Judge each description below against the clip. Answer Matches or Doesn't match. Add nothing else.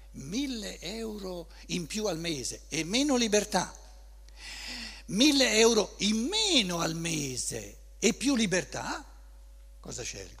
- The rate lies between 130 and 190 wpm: Doesn't match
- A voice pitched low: Doesn't match